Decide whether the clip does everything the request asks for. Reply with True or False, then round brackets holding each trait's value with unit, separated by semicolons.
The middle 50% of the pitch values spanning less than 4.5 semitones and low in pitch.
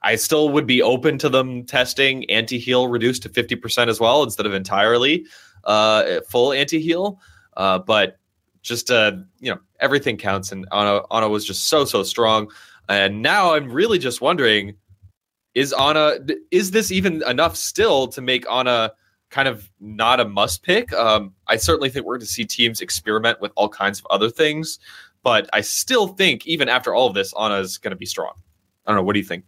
False (5.5 semitones; 115 Hz)